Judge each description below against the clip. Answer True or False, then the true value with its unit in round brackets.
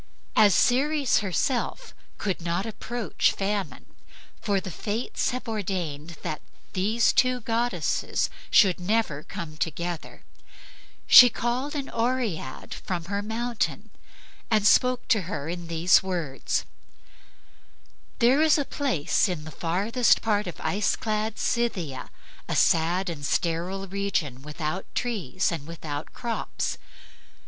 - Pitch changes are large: True (5.7 semitones)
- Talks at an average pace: False (120 wpm)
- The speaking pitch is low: False (195 Hz)